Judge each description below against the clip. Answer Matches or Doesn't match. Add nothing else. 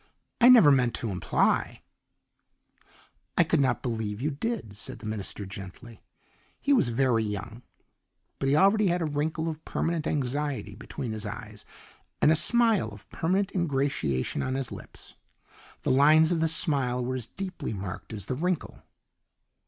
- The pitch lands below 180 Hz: Matches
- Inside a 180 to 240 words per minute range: Doesn't match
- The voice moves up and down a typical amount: Doesn't match